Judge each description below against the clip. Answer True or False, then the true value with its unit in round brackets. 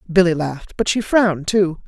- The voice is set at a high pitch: False (180 Hz)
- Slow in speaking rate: False (190 wpm)